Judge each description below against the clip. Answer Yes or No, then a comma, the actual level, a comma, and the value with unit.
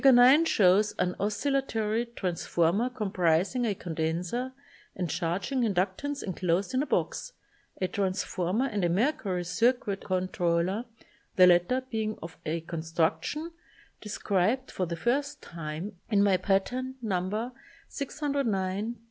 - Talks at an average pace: No, slow, 125 wpm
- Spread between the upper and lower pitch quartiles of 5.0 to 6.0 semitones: Yes, wide, 5.5 semitones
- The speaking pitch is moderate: No, high, 195 Hz